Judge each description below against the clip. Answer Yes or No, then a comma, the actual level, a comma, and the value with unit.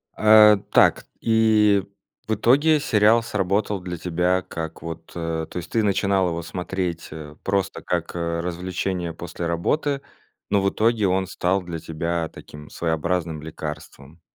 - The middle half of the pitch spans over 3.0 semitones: Yes, average, 3.7 semitones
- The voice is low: Yes, very low, 90 Hz